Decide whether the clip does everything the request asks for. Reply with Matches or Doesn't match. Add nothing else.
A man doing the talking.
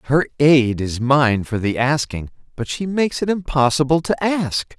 Matches